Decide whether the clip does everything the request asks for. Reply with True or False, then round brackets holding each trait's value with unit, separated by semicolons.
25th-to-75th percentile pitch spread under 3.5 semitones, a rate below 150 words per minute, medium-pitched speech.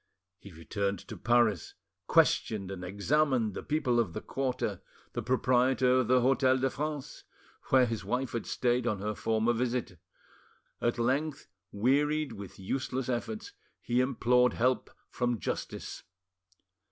False (3.1 semitones; 140 wpm; 125 Hz)